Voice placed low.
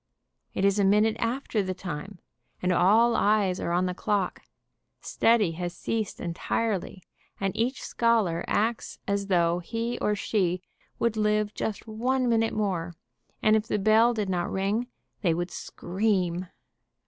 No: high, 205 Hz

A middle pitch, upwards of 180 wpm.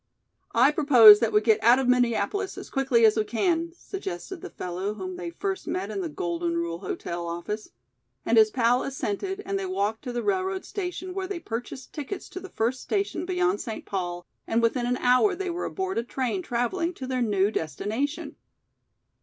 No: high, 245 Hz; average, 195 wpm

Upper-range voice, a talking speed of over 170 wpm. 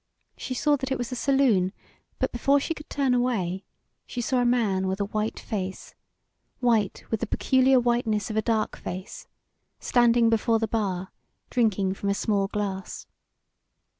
No: high, 225 Hz; average, 165 wpm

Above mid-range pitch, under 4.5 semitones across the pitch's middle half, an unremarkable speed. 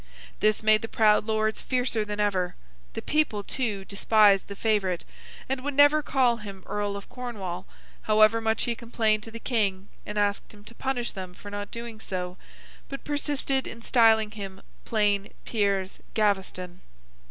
Yes: high, 215 Hz; narrow, 2.6 semitones; average, 165 wpm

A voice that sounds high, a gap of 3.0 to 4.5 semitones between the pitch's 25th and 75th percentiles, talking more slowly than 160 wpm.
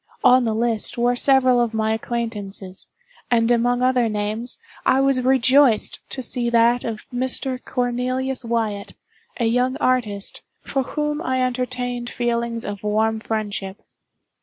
No: high, 240 Hz; narrow, 2.4 semitones; slow, 135 wpm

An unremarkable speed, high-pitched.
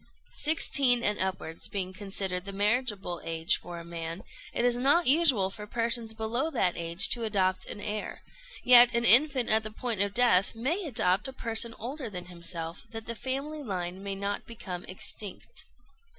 Yes: average, 175 wpm; high, 215 Hz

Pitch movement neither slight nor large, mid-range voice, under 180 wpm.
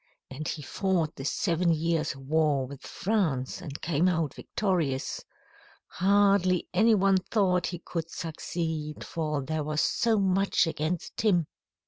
Yes: average, 3.7 semitones; medium, 165 Hz; slow, 135 wpm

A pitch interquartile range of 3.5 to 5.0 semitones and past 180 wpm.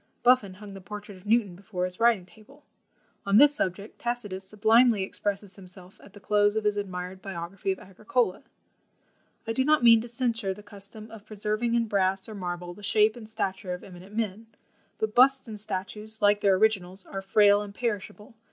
No: narrow, 2.6 semitones; average, 190 wpm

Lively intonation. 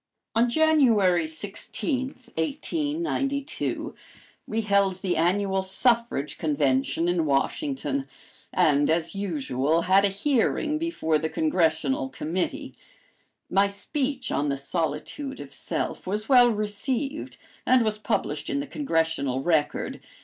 Yes: wide, 8.5 semitones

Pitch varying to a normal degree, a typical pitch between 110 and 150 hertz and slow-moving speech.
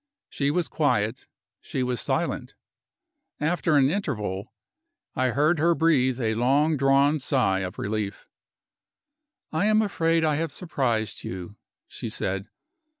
No: wide, 6.3 semitones; low, 135 Hz; slow, 130 wpm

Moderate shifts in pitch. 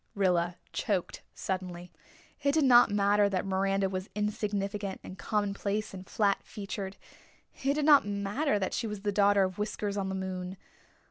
No: narrow, 1.6 semitones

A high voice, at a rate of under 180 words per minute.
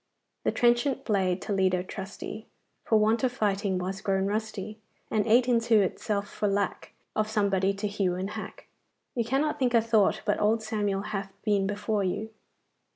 Yes: high, 210 Hz; average, 165 wpm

